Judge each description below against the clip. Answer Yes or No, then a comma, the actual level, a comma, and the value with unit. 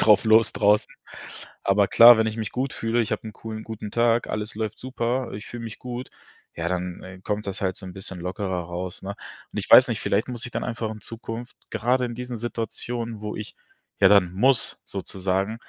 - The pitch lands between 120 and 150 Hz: No, low, 110 Hz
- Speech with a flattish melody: No, average, 3.2 semitones